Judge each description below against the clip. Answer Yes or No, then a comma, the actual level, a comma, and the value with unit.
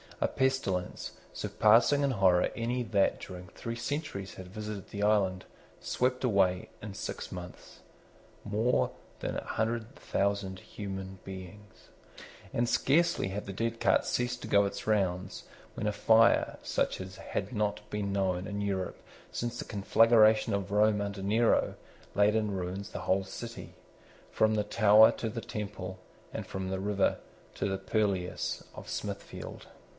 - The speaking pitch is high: No, low, 105 Hz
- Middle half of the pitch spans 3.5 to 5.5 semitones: No, average, 2.8 semitones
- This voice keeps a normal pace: Yes, average, 150 wpm